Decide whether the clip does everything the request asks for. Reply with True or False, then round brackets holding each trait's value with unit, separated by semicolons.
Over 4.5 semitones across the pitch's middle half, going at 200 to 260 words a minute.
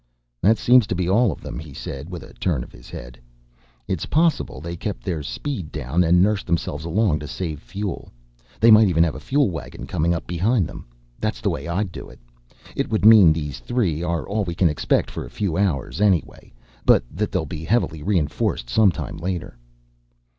True (5.0 semitones; 205 wpm)